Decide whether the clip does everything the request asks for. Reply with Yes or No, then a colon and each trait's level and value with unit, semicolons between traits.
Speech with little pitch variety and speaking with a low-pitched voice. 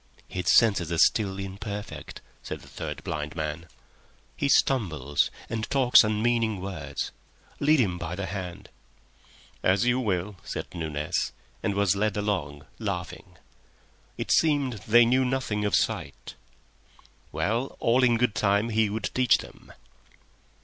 No: average, 4.5 semitones; low, 105 Hz